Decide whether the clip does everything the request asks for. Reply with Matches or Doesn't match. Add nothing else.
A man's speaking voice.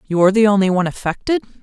Doesn't match